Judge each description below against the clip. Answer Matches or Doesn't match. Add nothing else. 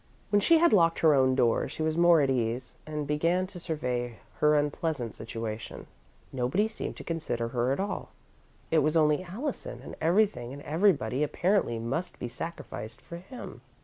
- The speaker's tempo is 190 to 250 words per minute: Doesn't match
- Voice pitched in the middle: Matches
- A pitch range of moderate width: Doesn't match